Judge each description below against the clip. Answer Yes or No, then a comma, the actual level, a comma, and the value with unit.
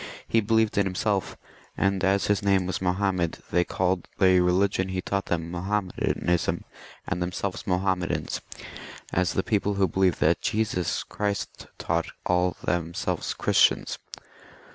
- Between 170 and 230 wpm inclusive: No, slow, 135 wpm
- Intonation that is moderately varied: No, narrow, 1.8 semitones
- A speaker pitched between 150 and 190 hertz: No, very low, 95 Hz